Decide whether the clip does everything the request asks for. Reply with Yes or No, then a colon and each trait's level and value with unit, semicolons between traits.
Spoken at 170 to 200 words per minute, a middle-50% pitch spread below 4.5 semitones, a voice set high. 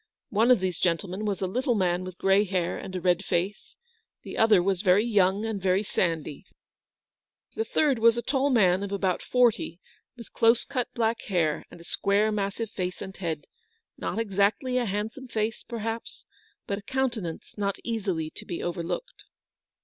Yes: average, 175 wpm; average, 3.8 semitones; high, 200 Hz